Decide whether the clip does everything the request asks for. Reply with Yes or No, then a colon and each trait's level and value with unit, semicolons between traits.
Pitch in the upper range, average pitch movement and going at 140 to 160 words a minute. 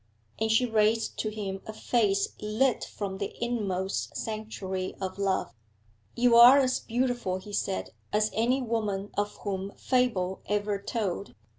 Yes: high, 210 Hz; average, 3.1 semitones; average, 145 wpm